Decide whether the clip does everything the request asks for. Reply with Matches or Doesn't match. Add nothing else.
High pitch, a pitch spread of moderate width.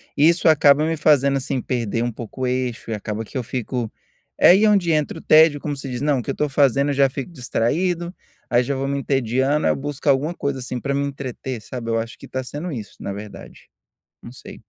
Doesn't match